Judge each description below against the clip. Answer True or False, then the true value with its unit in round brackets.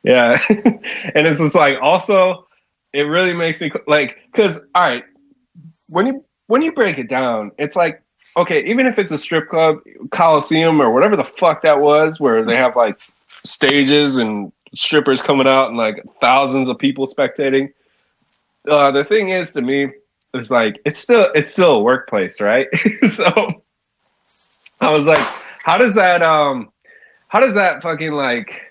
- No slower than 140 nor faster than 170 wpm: True (165 wpm)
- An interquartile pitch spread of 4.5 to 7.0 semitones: True (4.8 semitones)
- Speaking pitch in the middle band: True (155 Hz)